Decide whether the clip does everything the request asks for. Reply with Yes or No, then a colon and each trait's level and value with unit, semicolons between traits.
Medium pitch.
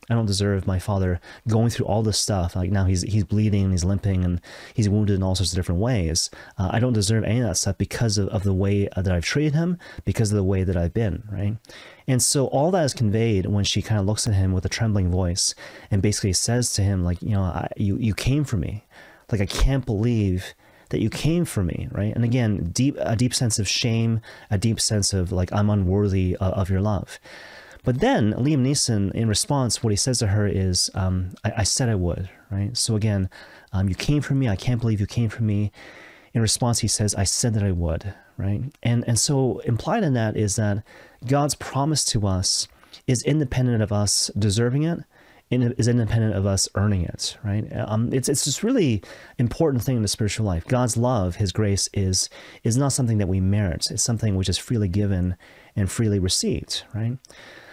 No: low, 105 Hz